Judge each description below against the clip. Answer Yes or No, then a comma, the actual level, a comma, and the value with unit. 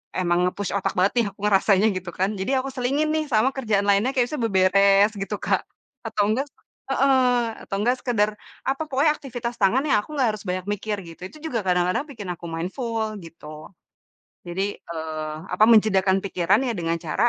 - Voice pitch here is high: Yes, high, 205 Hz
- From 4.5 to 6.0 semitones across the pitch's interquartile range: Yes, average, 5.1 semitones